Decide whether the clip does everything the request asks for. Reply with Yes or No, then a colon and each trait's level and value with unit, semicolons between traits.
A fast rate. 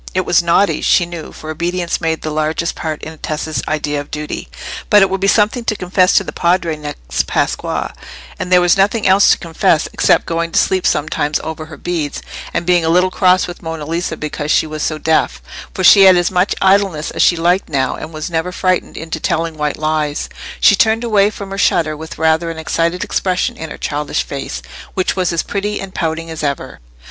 Yes: fast, 215 wpm